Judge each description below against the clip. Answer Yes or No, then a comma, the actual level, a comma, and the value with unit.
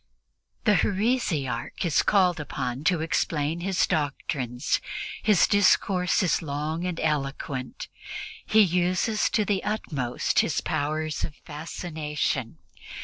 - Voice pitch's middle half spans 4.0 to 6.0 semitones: Yes, average, 4.4 semitones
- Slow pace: Yes, slow, 110 wpm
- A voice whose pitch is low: No, medium, 160 Hz